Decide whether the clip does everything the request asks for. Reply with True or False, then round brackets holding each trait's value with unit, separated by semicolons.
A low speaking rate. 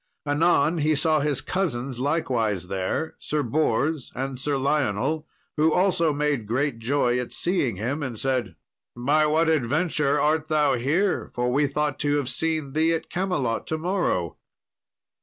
False (155 wpm)